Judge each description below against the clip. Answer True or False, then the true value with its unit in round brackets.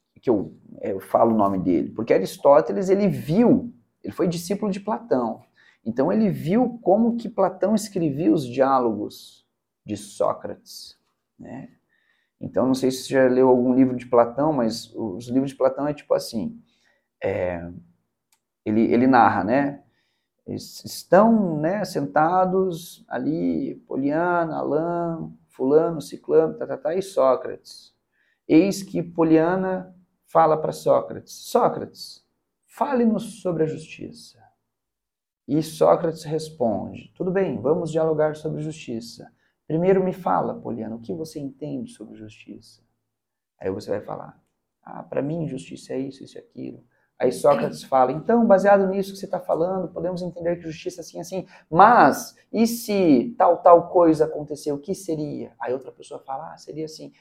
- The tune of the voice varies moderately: False (6.4 semitones)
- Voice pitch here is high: False (160 Hz)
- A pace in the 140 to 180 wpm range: True (150 wpm)